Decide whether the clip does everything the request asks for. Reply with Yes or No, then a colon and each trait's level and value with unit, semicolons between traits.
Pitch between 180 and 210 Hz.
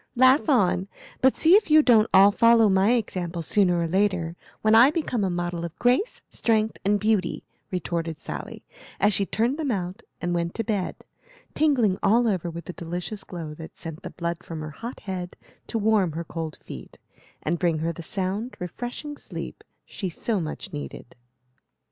Yes: high, 190 Hz